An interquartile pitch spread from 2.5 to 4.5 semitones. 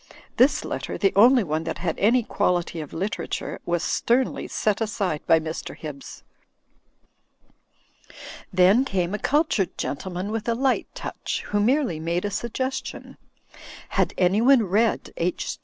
No: wide, 5.4 semitones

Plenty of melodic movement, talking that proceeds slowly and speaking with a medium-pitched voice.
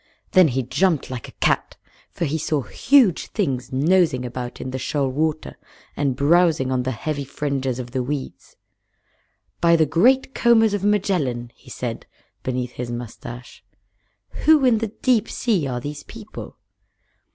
No: wide, 6.6 semitones; average, 155 wpm; medium, 145 Hz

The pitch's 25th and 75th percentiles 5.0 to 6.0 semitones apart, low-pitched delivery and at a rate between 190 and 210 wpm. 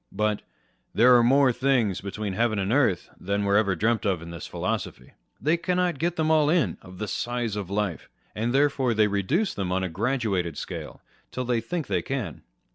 Yes: wide, 5.5 semitones; low, 110 Hz; average, 200 wpm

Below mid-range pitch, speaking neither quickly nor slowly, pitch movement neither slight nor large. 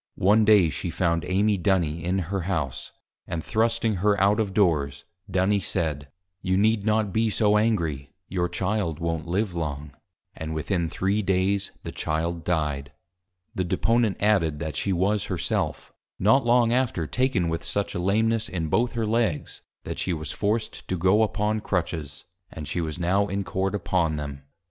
Yes: very low, 95 Hz; average, 170 wpm; average, 4.3 semitones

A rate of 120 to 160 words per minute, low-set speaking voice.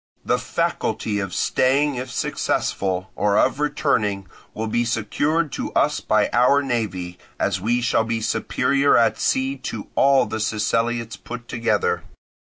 Yes: average, 145 wpm; low, 115 Hz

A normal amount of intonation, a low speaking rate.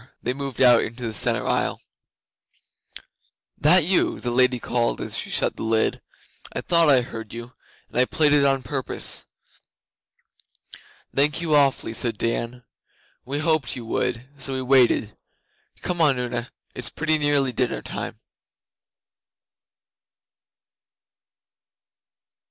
Yes: average, 3.5 semitones; slow, 130 wpm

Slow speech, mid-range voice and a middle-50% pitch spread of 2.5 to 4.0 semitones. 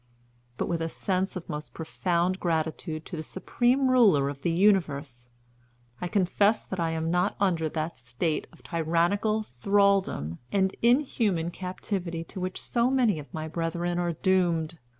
No: average, 155 wpm; medium, 175 Hz; average, 3.6 semitones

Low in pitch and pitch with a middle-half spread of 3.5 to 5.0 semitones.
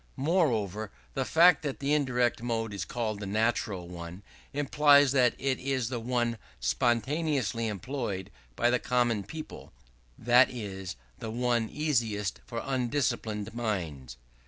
Yes: low, 120 Hz; average, 4.2 semitones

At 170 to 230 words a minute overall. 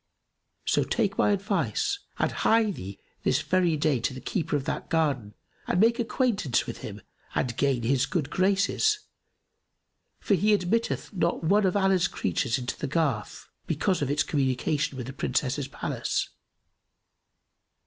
No: average, 150 wpm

